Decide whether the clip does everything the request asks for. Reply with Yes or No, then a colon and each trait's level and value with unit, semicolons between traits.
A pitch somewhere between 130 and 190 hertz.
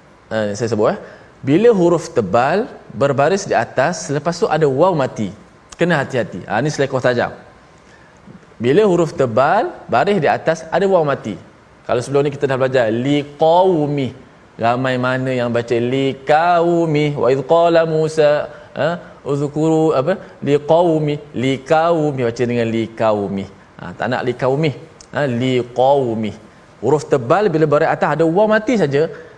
Yes: medium, 140 Hz